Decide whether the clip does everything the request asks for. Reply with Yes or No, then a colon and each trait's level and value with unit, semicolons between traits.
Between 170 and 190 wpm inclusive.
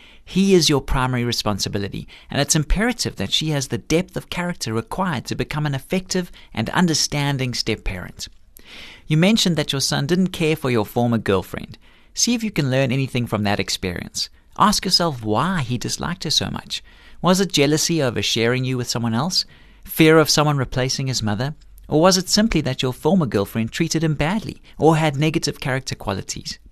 Yes: average, 185 wpm